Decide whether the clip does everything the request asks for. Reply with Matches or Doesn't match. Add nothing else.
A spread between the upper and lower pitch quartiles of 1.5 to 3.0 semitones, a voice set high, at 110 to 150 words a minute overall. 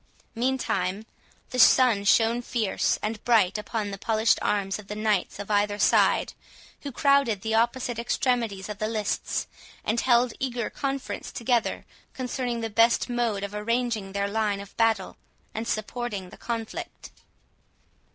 Matches